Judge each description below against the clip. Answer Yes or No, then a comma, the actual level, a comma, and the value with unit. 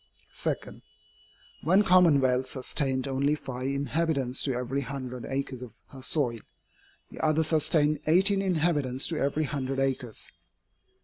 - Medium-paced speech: No, slow, 125 wpm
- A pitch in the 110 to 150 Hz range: Yes, medium, 140 Hz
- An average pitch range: Yes, average, 3.2 semitones